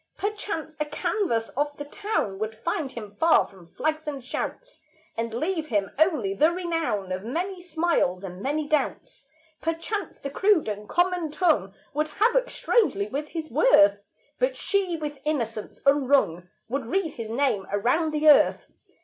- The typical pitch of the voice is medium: No, very high, 295 Hz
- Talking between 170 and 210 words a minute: No, average, 160 wpm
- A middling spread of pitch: No, wide, 7.3 semitones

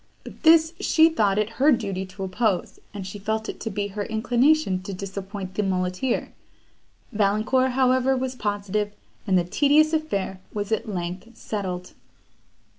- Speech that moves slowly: No, average, 155 wpm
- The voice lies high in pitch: Yes, high, 210 Hz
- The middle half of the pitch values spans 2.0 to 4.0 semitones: No, average, 4.8 semitones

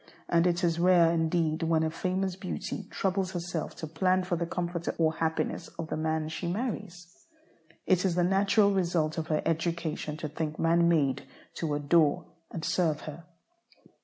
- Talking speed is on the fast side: No, average, 170 wpm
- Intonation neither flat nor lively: No, narrow, 2.1 semitones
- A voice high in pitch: No, medium, 170 Hz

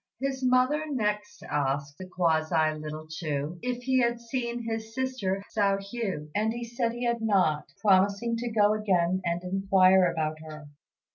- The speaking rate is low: No, average, 160 wpm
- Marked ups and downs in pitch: Yes, wide, 5.7 semitones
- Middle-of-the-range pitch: No, high, 200 Hz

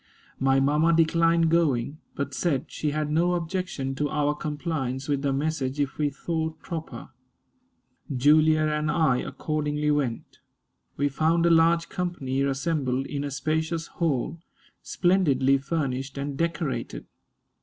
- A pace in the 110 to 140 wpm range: Yes, slow, 135 wpm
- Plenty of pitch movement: No, average, 3.0 semitones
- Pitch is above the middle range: No, medium, 150 Hz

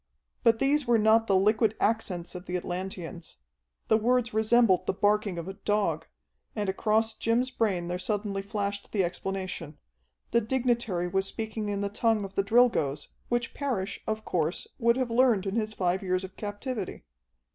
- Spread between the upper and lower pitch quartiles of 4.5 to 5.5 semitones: No, average, 3.3 semitones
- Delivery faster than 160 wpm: Yes, average, 170 wpm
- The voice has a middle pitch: No, high, 205 Hz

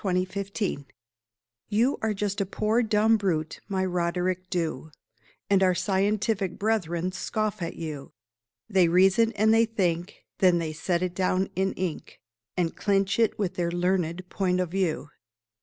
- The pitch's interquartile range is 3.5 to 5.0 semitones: No, average, 2.8 semitones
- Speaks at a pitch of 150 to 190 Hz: Yes, medium, 185 Hz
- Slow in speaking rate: No, average, 155 wpm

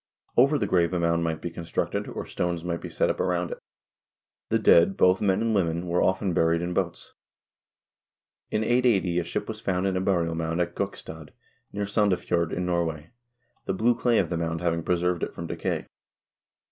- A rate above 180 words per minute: Yes, average, 195 wpm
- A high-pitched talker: No, very low, 90 Hz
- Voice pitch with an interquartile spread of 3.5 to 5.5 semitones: No, narrow, 2.5 semitones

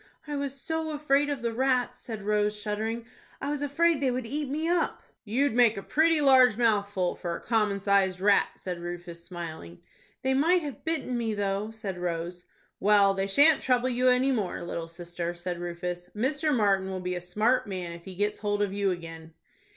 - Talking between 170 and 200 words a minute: Yes, average, 195 wpm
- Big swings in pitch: Yes, wide, 6.5 semitones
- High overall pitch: Yes, high, 210 Hz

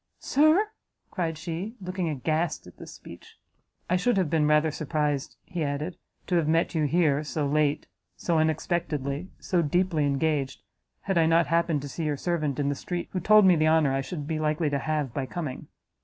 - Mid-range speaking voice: Yes, medium, 155 Hz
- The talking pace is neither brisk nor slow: Yes, average, 195 wpm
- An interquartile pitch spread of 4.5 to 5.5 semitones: No, average, 3.0 semitones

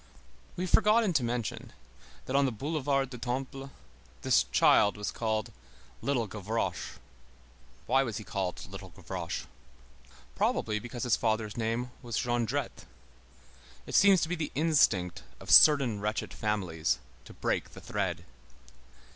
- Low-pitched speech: Yes, low, 120 Hz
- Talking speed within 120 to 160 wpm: Yes, average, 140 wpm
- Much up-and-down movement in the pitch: No, average, 4.4 semitones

